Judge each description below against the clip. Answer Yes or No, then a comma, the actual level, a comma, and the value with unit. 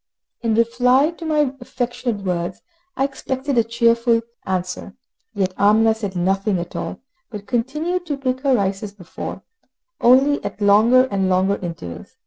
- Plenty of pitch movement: No, average, 5.0 semitones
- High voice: Yes, high, 230 Hz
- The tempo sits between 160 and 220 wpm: No, average, 150 wpm